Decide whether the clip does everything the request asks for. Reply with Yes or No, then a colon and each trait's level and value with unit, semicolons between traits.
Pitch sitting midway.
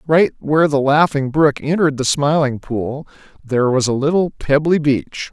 Yes: medium, 145 Hz